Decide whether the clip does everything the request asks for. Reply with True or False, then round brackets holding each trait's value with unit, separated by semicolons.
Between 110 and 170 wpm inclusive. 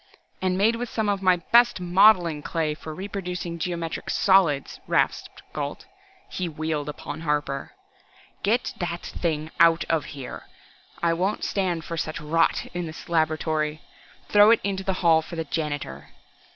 True (150 wpm)